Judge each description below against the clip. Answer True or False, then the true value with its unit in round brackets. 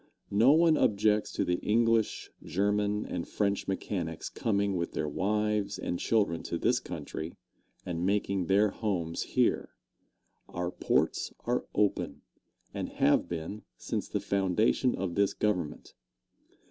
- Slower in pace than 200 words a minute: True (135 wpm)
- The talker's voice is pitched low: True (100 Hz)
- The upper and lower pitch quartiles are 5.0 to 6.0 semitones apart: False (3.2 semitones)